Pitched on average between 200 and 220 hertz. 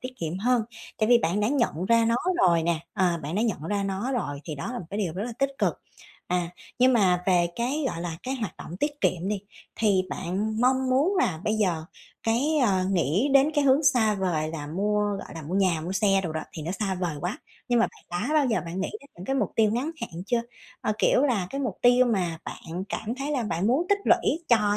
Yes: high, 205 Hz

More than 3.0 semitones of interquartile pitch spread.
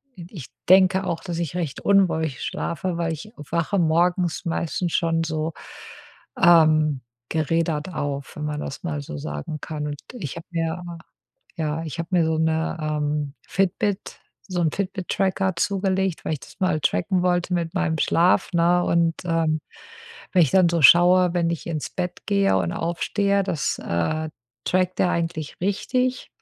No: average, 2.7 semitones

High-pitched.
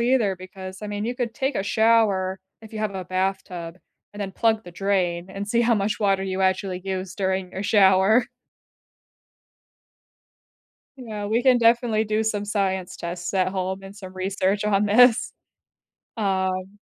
Yes: high, 195 Hz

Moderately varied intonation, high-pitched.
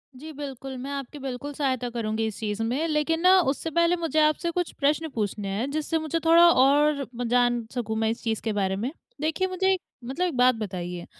No: wide, 5.7 semitones; very high, 275 Hz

